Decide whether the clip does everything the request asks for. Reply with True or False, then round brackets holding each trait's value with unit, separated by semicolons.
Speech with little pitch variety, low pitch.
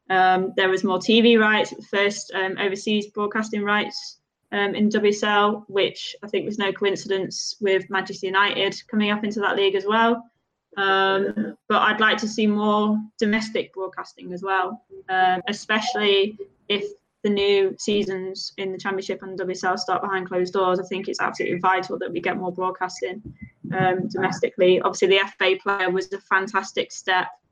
False (1.8 semitones; 195 Hz)